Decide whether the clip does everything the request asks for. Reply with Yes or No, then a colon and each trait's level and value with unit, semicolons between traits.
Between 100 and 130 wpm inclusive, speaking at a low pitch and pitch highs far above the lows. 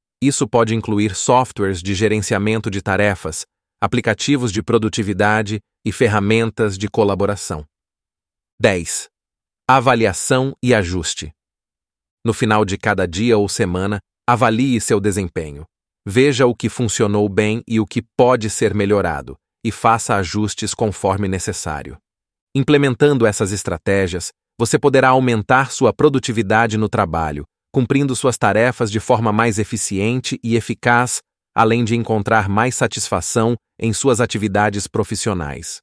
No: slow, 120 wpm; low, 110 Hz; average, 3.2 semitones